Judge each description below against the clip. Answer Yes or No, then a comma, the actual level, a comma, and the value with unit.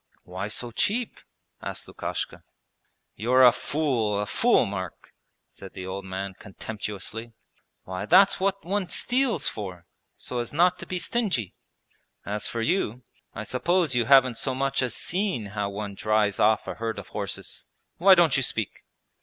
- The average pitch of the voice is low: Yes, low, 120 Hz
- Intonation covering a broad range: Yes, wide, 8.8 semitones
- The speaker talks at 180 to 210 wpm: No, average, 160 wpm